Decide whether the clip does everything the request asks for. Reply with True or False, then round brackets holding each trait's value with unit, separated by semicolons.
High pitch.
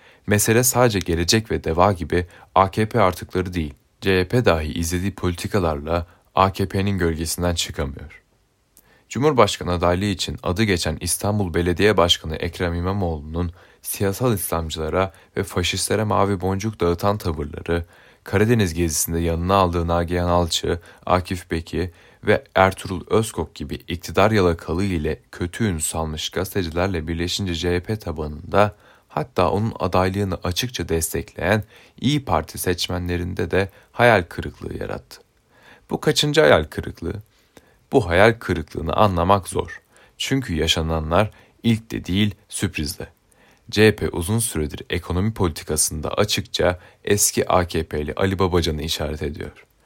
False (90 Hz)